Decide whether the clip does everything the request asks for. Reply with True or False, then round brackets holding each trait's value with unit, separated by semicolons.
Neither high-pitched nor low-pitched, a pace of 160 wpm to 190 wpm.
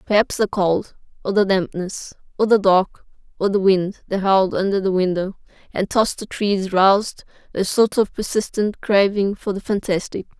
False (195 Hz; 175 wpm)